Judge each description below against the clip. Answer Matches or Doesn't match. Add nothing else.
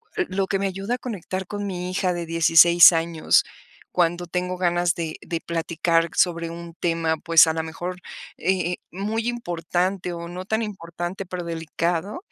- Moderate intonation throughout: Doesn't match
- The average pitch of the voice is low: Doesn't match